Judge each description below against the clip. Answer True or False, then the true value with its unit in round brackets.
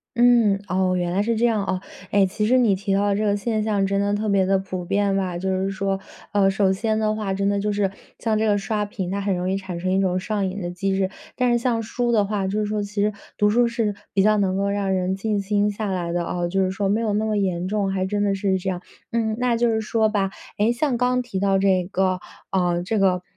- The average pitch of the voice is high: True (200 Hz)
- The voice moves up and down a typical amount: False (2.0 semitones)